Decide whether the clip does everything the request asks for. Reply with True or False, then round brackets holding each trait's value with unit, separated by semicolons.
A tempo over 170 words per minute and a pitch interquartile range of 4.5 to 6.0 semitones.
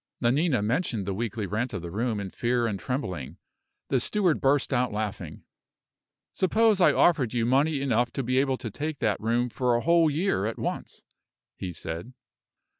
True (180 wpm; 4.8 semitones)